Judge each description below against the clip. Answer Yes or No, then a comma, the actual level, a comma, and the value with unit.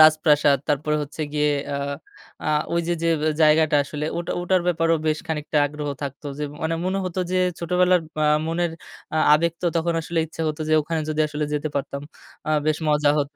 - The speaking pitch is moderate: Yes, medium, 155 Hz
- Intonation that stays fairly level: Yes, narrow, 2.1 semitones